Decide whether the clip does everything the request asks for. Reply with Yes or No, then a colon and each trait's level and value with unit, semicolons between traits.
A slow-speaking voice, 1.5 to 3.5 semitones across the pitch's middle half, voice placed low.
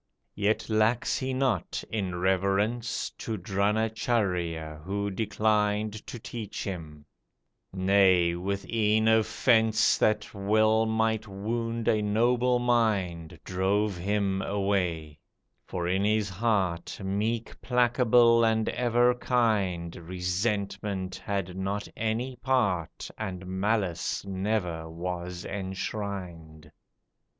Yes: slow, 100 wpm; average, 3.2 semitones; low, 100 Hz